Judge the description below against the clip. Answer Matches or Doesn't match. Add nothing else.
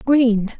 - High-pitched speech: Matches